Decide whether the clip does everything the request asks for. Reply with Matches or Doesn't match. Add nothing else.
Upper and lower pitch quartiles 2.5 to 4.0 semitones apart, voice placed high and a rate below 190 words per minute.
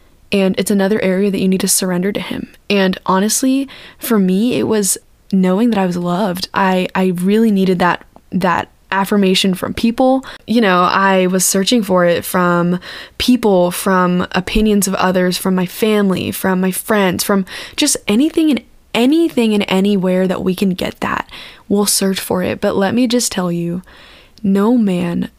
Matches